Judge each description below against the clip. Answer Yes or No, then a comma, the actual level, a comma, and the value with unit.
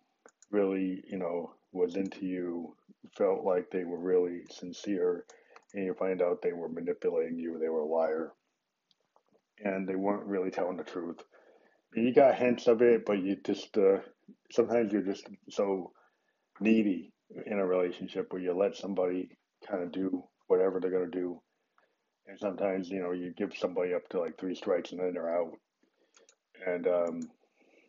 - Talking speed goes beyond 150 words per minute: Yes, average, 170 wpm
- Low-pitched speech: Yes, very low, 95 Hz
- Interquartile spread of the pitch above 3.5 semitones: No, narrow, 2.4 semitones